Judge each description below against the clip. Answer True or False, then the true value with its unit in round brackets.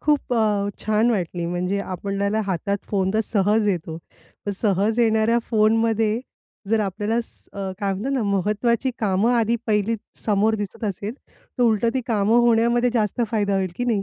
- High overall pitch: True (215 Hz)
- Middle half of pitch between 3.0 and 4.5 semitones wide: False (2.5 semitones)